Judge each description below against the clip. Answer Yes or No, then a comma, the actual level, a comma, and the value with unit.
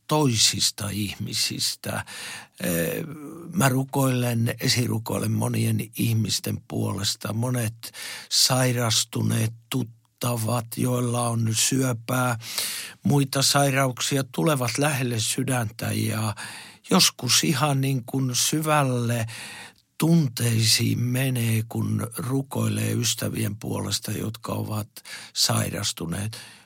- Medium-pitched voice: No, low, 120 Hz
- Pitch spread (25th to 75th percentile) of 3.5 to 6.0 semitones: No, average, 3.1 semitones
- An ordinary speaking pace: No, slow, 75 wpm